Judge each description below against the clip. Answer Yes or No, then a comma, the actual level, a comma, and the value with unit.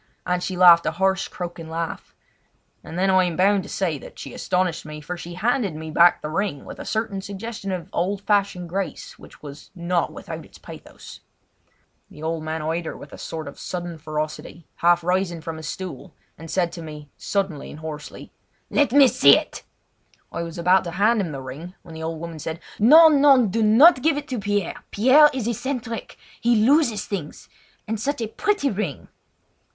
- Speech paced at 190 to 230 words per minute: Yes, average, 195 wpm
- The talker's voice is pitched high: No, medium, 180 Hz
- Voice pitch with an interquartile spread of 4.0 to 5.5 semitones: Yes, average, 4.7 semitones